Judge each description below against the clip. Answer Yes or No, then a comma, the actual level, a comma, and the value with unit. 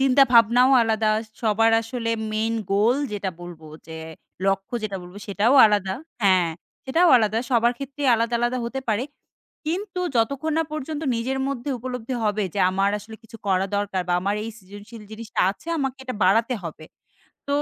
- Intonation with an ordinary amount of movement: Yes, average, 4.2 semitones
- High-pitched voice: Yes, high, 225 Hz